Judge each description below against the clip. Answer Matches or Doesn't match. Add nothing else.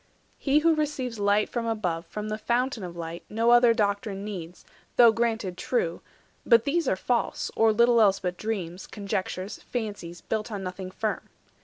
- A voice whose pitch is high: Matches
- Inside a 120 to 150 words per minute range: Doesn't match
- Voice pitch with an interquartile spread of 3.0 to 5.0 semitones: Matches